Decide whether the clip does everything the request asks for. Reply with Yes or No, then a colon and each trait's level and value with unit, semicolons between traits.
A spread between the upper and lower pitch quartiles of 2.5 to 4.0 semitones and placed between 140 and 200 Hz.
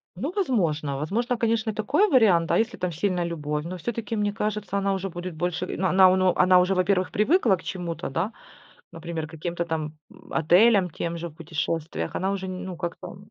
Yes: average, 3.7 semitones; medium, 185 Hz